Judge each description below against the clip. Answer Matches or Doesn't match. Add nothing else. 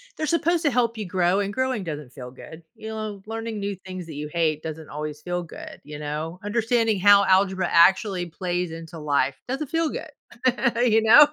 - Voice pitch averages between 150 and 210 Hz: Matches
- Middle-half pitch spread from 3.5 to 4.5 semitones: Doesn't match